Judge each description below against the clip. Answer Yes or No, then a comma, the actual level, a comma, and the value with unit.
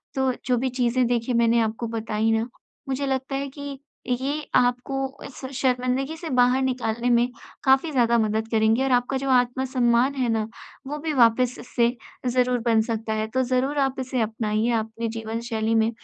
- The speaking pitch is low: No, high, 245 Hz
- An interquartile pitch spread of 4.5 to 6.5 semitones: No, narrow, 2.6 semitones